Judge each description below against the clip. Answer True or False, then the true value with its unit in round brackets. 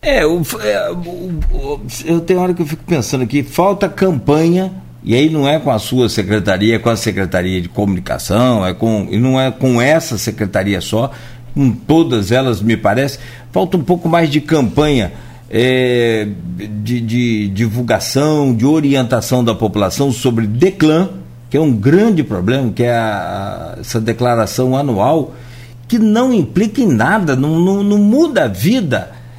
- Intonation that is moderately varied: False (5.9 semitones)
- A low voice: True (125 Hz)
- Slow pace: False (165 wpm)